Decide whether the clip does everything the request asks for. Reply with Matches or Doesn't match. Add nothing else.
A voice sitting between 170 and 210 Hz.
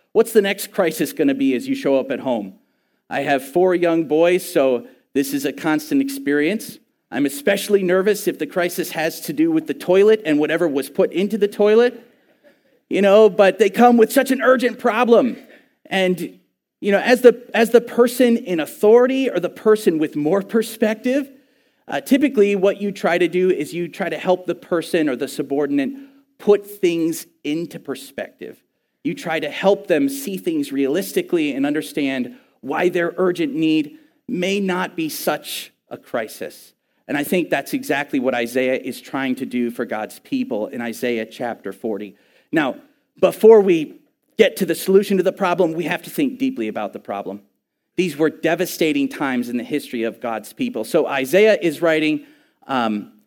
Matches